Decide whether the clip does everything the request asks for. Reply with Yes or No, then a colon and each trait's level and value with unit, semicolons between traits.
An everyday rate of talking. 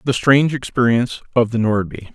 Yes: average, 170 wpm